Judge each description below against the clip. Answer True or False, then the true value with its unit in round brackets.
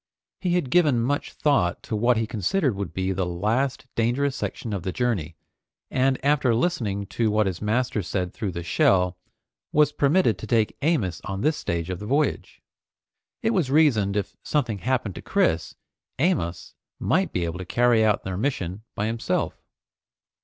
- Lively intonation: True (6.4 semitones)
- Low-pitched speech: True (110 Hz)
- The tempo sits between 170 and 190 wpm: True (175 wpm)